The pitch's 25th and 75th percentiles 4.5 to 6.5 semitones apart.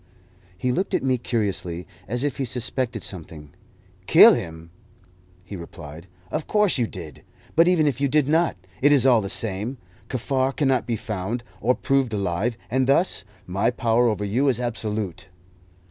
Yes: average, 5.3 semitones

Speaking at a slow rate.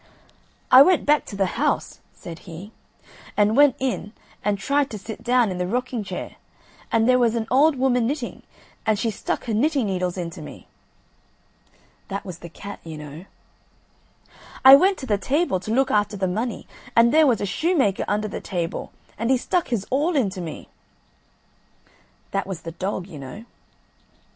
No: average, 175 wpm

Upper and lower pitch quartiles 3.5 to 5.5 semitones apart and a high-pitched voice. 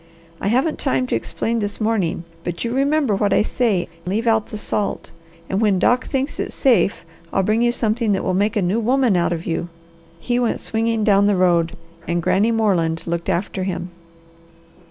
Yes: average, 4.3 semitones; high, 205 Hz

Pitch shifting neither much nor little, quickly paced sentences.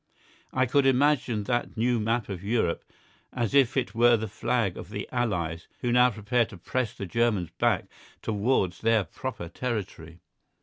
No: average, 3.7 semitones; average, 165 wpm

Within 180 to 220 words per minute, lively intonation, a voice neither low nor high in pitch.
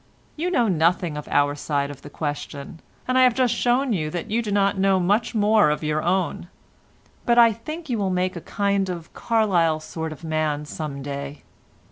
Yes: fast, 205 wpm; wide, 6.3 semitones; medium, 180 Hz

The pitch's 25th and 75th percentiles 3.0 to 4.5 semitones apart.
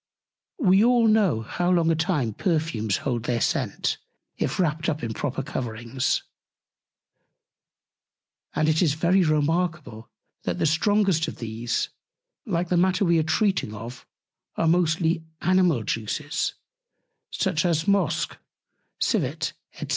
No: wide, 5.6 semitones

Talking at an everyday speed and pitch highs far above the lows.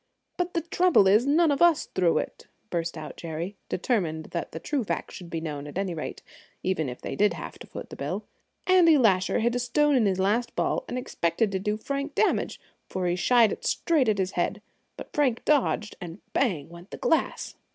No: fast, 215 wpm; wide, 8.1 semitones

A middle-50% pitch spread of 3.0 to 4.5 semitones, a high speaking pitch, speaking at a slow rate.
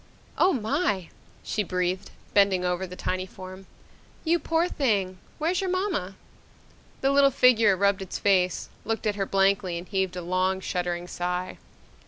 No: average, 3.6 semitones; high, 195 Hz; average, 155 wpm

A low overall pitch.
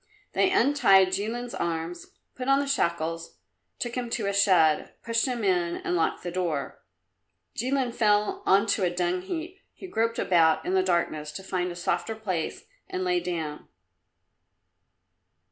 No: high, 190 Hz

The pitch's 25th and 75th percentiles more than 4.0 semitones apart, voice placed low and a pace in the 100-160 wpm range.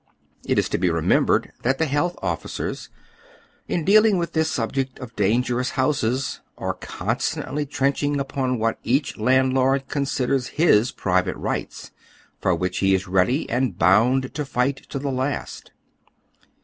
No: average, 3.7 semitones; low, 130 Hz; average, 150 wpm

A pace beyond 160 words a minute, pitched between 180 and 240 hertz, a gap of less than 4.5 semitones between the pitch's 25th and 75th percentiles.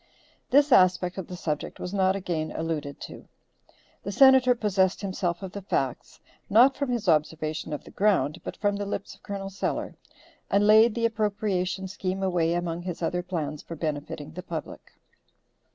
Yes: average, 170 wpm; medium, 185 Hz; average, 3.7 semitones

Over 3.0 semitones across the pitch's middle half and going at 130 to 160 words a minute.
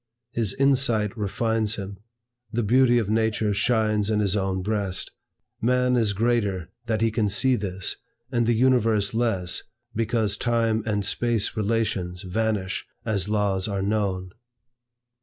No: narrow, 2.6 semitones; average, 140 wpm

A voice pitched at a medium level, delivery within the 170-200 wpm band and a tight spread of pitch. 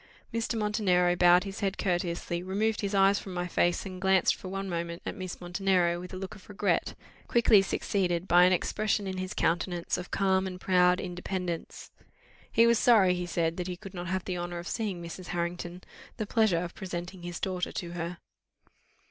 Yes: medium, 180 Hz; average, 195 wpm; narrow, 1.9 semitones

